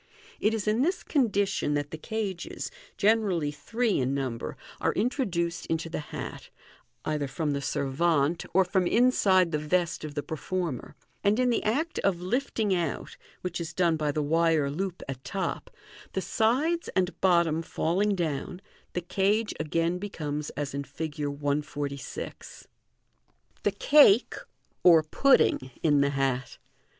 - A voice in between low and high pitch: Yes, medium, 170 Hz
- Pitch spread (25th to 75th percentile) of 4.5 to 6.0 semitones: Yes, wide, 5.4 semitones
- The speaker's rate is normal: Yes, average, 150 wpm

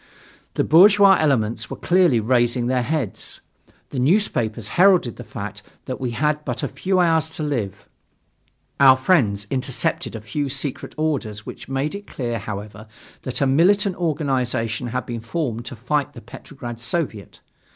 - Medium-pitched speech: No, low, 130 Hz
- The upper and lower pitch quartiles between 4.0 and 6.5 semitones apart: Yes, average, 5.1 semitones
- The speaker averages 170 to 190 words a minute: No, average, 160 wpm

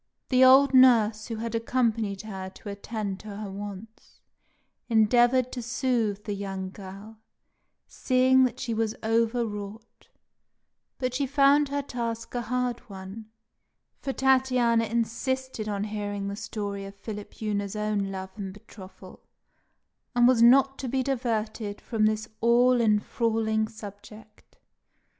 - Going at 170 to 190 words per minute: No, slow, 135 wpm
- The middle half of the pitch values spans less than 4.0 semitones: Yes, average, 3.2 semitones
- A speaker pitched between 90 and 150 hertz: No, high, 225 Hz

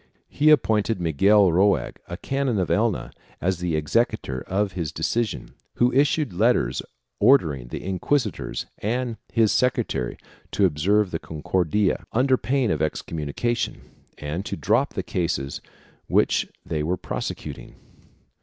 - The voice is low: Yes, very low, 95 Hz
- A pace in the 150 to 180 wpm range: No, slow, 135 wpm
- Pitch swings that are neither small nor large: No, wide, 6.5 semitones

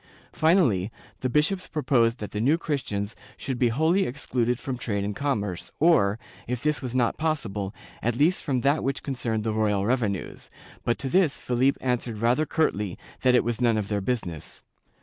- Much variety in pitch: No, average, 4.8 semitones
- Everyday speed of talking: Yes, average, 180 wpm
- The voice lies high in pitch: No, low, 125 Hz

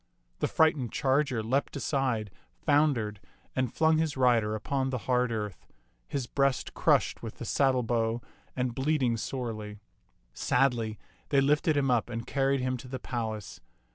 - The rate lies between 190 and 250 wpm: No, average, 150 wpm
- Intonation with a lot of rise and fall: No, average, 3.2 semitones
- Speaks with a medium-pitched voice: No, low, 130 Hz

